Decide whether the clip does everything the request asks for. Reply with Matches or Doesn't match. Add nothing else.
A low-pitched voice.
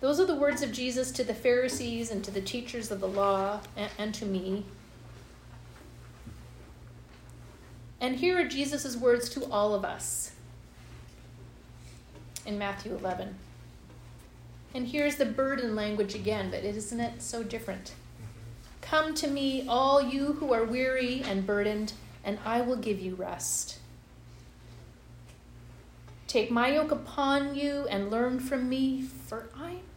Doesn't match